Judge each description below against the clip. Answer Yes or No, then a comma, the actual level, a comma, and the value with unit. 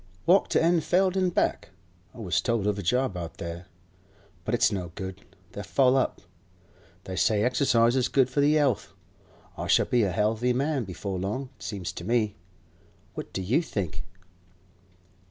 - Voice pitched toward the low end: Yes, low, 115 Hz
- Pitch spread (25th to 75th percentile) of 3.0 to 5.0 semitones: No, wide, 5.6 semitones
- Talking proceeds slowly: No, average, 175 wpm